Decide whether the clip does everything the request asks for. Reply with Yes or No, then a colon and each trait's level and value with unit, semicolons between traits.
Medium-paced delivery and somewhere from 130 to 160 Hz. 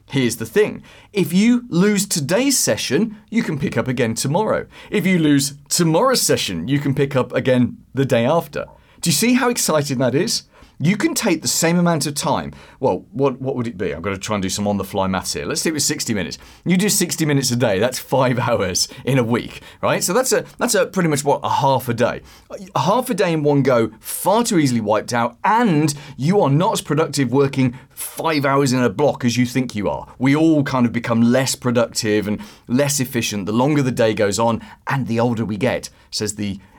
No: fast, 230 wpm; medium, 140 Hz